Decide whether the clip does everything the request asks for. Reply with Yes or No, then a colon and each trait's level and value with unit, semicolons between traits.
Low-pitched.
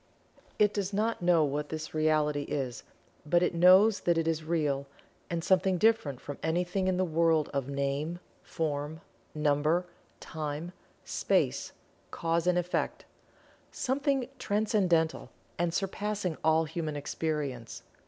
No: medium, 165 Hz